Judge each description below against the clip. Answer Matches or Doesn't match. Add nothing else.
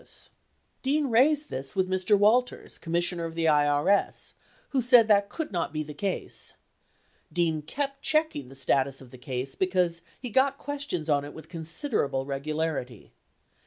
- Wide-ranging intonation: Matches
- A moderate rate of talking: Matches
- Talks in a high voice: Doesn't match